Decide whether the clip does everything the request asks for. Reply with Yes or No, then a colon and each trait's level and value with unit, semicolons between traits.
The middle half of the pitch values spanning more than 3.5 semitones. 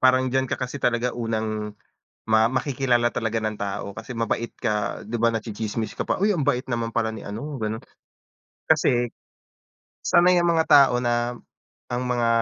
No: average, 2.7 semitones